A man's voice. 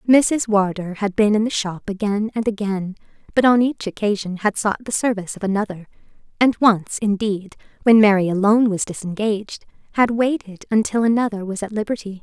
No: female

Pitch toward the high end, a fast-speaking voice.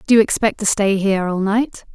Yes: high, 205 Hz; fast, 245 wpm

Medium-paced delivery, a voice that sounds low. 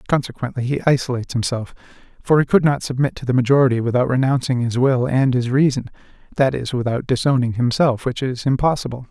Yes: average, 170 wpm; low, 130 Hz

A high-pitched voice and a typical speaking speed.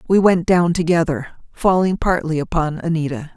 No: medium, 165 Hz; average, 145 wpm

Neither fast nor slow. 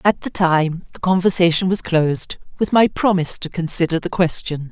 Yes: average, 180 wpm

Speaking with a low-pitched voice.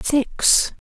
No: very high, 265 Hz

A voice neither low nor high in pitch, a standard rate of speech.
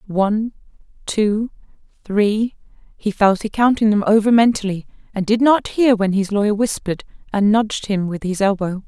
No: high, 210 Hz; average, 155 wpm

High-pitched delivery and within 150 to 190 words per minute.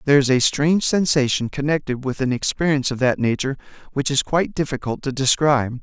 No: medium, 140 Hz; average, 185 wpm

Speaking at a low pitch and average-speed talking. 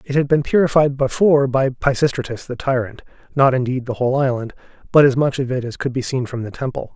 No: low, 130 Hz; fast, 225 wpm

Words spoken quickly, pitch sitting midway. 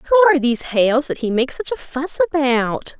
No: fast, 220 wpm; very high, 270 Hz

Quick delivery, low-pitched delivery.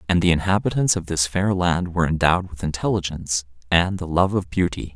No: average, 195 wpm; very low, 90 Hz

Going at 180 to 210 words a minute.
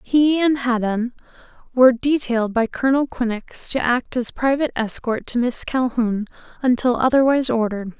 No: average, 145 wpm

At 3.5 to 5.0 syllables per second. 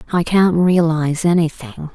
Yes: 4.8 syllables/s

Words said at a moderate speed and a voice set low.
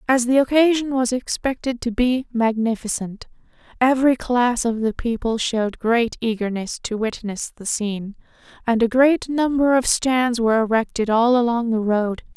No: average, 155 wpm; high, 240 Hz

